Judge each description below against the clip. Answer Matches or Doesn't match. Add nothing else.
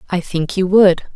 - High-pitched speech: Doesn't match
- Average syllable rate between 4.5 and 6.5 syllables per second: Matches